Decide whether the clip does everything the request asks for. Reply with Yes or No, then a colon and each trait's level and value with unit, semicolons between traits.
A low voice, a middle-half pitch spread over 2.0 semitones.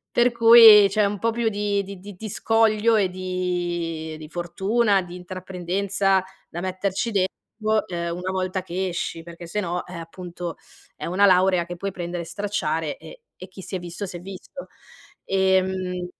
No: medium, 185 Hz; narrow, 2.4 semitones